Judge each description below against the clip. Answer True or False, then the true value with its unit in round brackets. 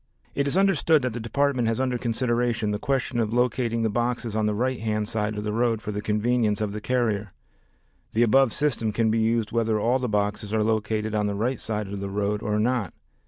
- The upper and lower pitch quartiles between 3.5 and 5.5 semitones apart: False (2.6 semitones)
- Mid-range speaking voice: False (110 Hz)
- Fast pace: True (225 wpm)